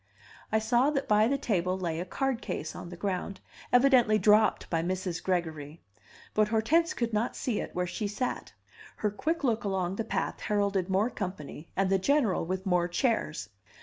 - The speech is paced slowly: No, average, 180 wpm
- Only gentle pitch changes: No, average, 4.5 semitones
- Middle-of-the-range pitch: No, high, 205 Hz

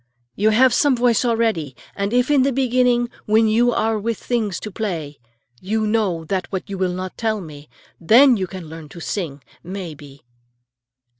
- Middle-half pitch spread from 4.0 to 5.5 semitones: Yes, average, 5.0 semitones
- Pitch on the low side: No, high, 210 Hz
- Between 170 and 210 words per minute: Yes, average, 180 wpm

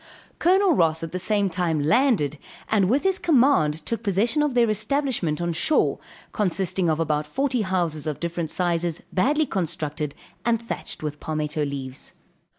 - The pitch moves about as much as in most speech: No, wide, 7.3 semitones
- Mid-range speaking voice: Yes, medium, 180 Hz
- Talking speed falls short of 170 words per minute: Yes, average, 155 wpm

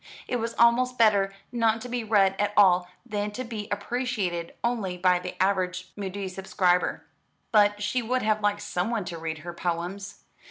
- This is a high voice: Yes, high, 205 Hz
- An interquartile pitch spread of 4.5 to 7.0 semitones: No, average, 3.9 semitones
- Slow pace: No, average, 170 wpm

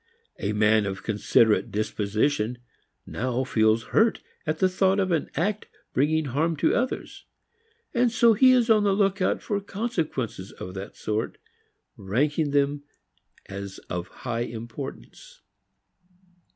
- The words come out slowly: Yes, slow, 130 wpm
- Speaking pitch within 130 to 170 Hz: Yes, medium, 140 Hz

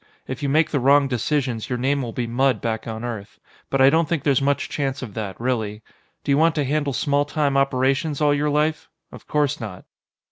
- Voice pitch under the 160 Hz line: Yes, low, 135 Hz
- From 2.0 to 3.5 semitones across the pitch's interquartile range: Yes, average, 3.0 semitones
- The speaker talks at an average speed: No, fast, 220 wpm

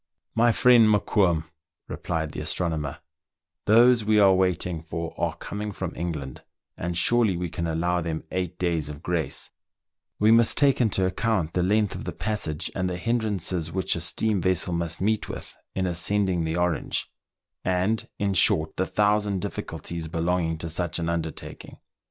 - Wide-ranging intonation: No, average, 3.8 semitones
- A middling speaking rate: Yes, average, 170 wpm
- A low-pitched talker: Yes, very low, 90 Hz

